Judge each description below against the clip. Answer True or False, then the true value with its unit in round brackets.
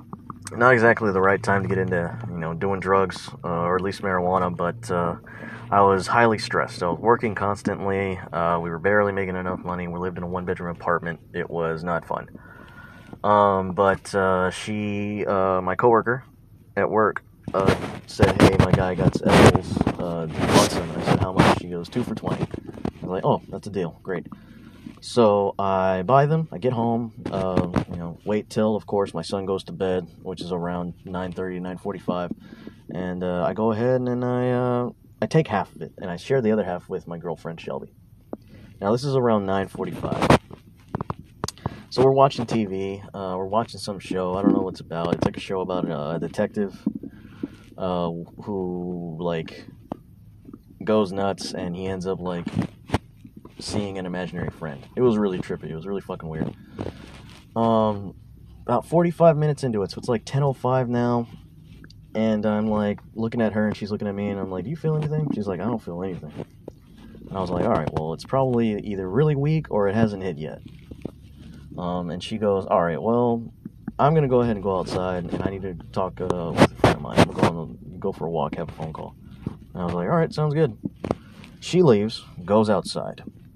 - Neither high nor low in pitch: False (100 Hz)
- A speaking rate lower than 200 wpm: False (205 wpm)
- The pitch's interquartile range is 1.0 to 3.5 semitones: False (4.1 semitones)